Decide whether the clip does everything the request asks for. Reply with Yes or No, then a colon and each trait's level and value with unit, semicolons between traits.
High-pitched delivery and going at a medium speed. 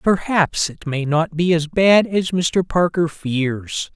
No: medium, 165 Hz; average, 165 wpm